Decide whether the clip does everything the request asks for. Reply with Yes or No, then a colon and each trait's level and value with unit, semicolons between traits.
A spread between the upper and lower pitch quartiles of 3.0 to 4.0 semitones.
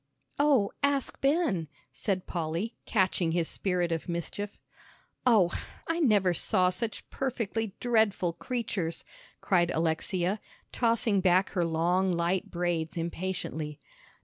No: average, 4.5 semitones